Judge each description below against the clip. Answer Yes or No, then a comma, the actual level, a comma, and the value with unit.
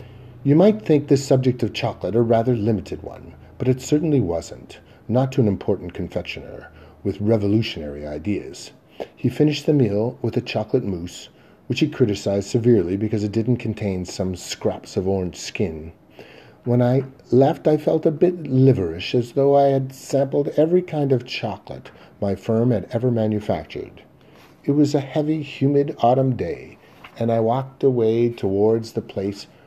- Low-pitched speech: Yes, low, 120 Hz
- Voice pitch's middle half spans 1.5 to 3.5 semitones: No, average, 4.8 semitones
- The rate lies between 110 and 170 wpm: Yes, average, 160 wpm